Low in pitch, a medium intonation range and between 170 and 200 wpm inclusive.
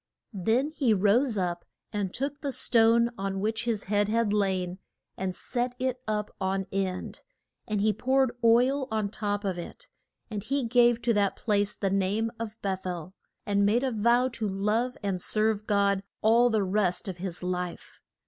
No: high, 210 Hz; average, 3.3 semitones; average, 175 wpm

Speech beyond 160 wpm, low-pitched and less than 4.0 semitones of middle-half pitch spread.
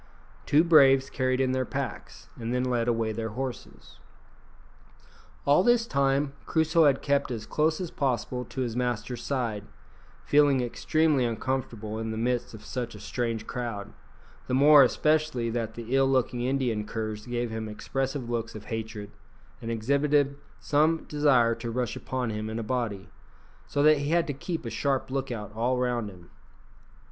Yes: average, 170 wpm; low, 125 Hz; average, 3.5 semitones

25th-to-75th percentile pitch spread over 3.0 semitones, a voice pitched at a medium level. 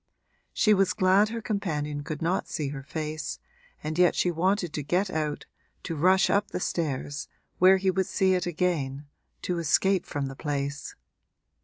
Yes: average, 4.2 semitones; medium, 170 Hz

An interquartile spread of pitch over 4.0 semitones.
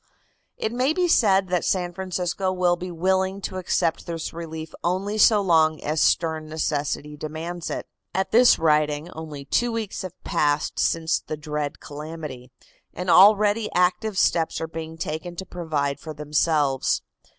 No: average, 3.4 semitones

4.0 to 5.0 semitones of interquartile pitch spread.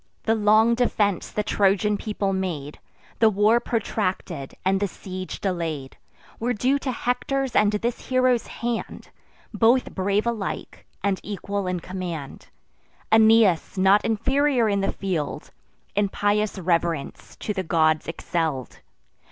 No: average, 3.5 semitones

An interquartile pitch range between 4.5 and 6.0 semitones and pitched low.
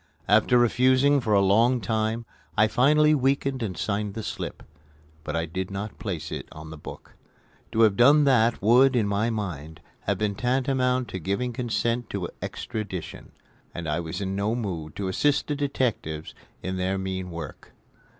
Yes: average, 5.0 semitones; low, 110 Hz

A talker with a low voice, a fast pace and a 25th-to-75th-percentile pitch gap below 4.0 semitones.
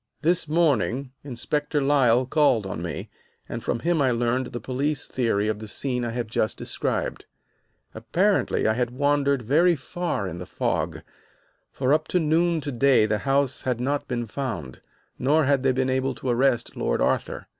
No: low, 130 Hz; average, 175 wpm; average, 3.6 semitones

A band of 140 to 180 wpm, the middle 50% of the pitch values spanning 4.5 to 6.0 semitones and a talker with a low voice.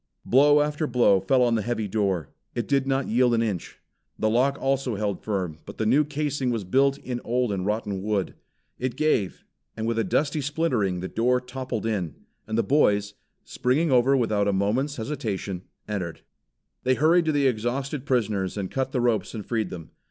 No: average, 190 wpm; average, 4.8 semitones; low, 120 Hz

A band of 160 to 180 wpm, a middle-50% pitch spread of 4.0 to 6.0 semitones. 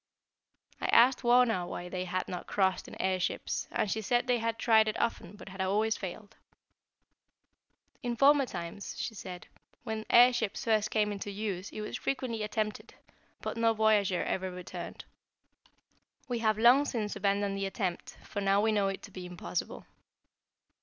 No: average, 170 wpm; average, 3.2 semitones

